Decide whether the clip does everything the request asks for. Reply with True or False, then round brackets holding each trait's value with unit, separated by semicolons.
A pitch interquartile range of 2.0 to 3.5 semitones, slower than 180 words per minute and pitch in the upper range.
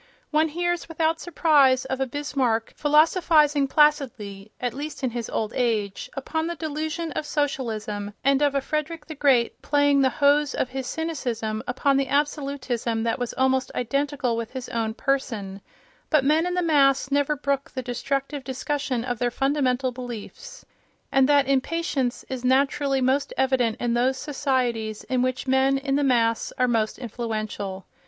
True (3.2 semitones; 160 wpm; 270 Hz)